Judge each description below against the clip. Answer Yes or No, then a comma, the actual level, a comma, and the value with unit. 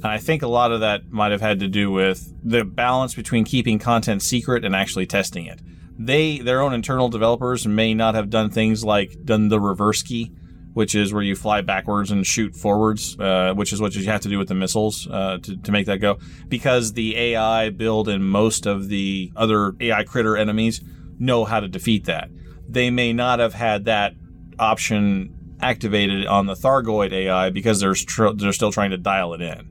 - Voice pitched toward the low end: Yes, low, 105 Hz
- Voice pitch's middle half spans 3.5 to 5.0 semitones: No, average, 2.7 semitones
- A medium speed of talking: No, fast, 210 wpm